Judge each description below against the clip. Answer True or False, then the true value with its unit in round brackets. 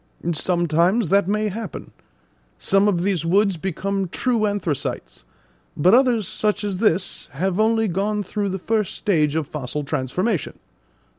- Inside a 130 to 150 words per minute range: True (140 wpm)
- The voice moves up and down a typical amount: True (3.9 semitones)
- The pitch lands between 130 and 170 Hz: False (195 Hz)